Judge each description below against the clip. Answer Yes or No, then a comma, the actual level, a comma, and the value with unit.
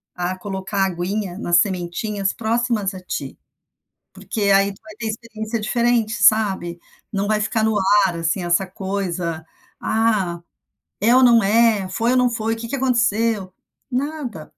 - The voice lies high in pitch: Yes, high, 210 Hz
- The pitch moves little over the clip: No, average, 3.5 semitones